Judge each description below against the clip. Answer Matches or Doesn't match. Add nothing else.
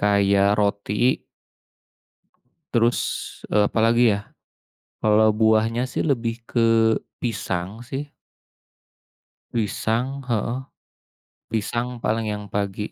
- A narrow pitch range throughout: Matches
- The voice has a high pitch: Doesn't match